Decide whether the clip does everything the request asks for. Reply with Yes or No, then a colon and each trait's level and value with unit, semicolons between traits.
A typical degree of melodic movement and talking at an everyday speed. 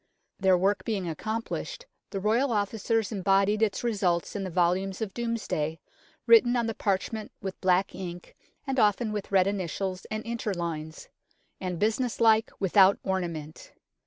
Yes: average, 3.2 semitones; average, 145 wpm